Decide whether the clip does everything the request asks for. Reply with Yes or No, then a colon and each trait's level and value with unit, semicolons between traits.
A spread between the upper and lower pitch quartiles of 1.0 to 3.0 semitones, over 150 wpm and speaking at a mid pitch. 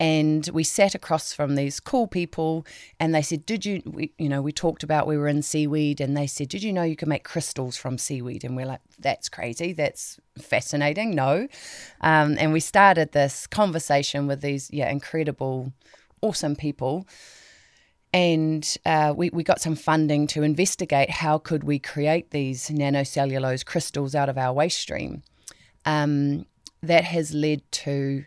Yes: narrow, 2.4 semitones; average, 170 wpm; medium, 150 Hz